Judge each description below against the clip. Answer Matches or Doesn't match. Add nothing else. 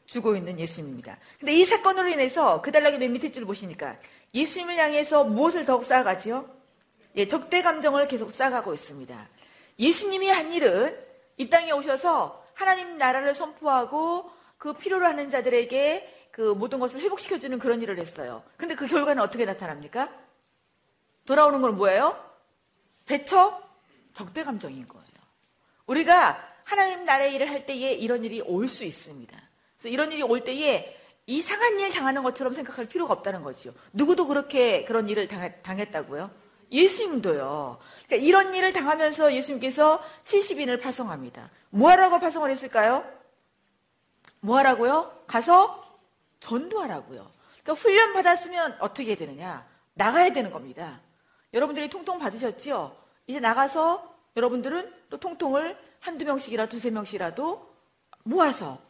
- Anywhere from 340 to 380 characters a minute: Matches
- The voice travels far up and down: Matches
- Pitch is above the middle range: Matches